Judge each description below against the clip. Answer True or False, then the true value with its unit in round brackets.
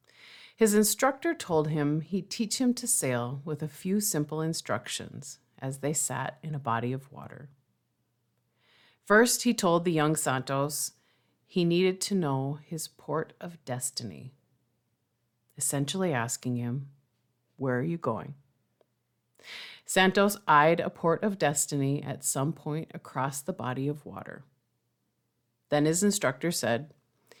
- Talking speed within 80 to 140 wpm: True (135 wpm)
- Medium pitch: True (150 Hz)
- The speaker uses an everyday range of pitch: True (4.6 semitones)